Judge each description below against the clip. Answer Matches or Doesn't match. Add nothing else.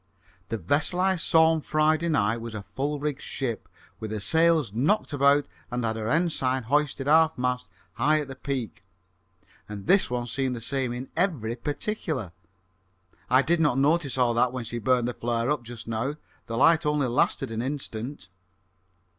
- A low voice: Matches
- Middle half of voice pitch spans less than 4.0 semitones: Doesn't match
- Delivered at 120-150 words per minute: Doesn't match